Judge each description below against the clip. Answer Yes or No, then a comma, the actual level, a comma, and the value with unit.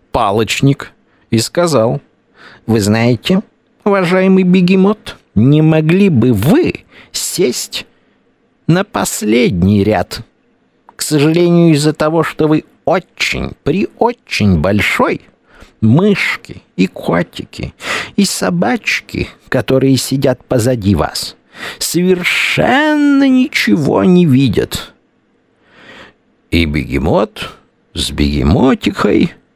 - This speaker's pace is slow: Yes, slow, 85 wpm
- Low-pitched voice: No, medium, 150 Hz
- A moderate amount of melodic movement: No, wide, 8.8 semitones